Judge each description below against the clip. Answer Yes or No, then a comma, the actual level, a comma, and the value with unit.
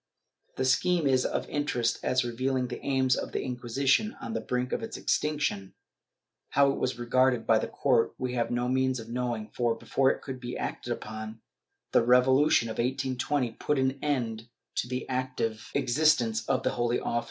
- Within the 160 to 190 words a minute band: Yes, average, 185 wpm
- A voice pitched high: No, low, 125 Hz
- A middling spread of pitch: No, narrow, 2.0 semitones